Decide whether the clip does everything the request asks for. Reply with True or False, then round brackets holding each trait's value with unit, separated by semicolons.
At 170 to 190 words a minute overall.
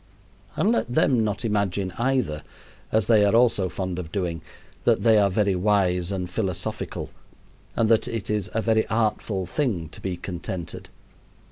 False (160 wpm)